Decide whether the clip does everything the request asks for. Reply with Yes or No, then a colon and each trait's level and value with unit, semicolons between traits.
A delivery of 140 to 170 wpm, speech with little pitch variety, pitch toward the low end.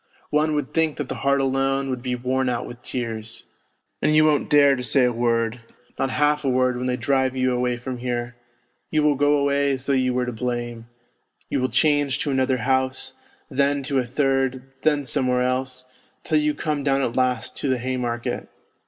No: fast, 205 wpm; narrow, 2.1 semitones; low, 130 Hz